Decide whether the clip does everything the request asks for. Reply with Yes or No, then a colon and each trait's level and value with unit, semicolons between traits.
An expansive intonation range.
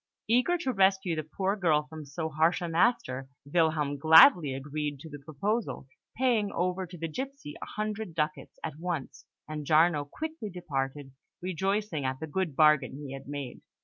No: average, 4.8 semitones